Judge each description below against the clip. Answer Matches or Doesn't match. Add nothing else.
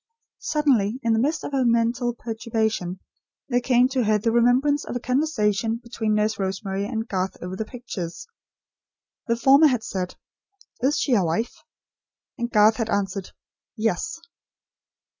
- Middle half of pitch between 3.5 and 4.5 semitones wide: Doesn't match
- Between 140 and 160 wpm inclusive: Matches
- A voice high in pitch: Matches